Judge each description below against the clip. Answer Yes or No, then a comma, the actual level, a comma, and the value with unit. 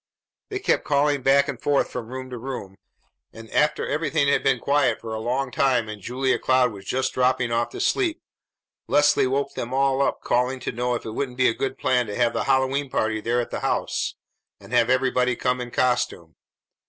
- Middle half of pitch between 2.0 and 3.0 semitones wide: Yes, narrow, 2.5 semitones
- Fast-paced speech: Yes, fast, 210 wpm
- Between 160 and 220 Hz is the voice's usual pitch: No, low, 130 Hz